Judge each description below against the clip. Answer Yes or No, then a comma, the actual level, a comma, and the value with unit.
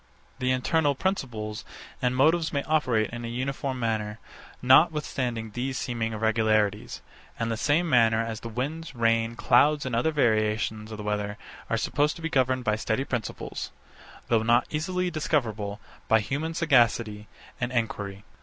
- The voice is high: No, low, 120 Hz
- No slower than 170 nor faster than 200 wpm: No, average, 155 wpm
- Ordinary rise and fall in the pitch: Yes, average, 4.2 semitones